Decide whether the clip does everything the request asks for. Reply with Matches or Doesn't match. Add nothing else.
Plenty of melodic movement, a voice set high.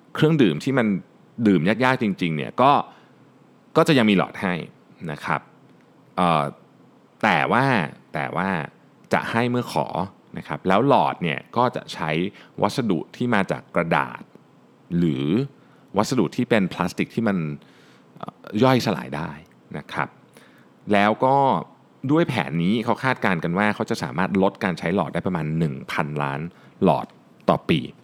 Doesn't match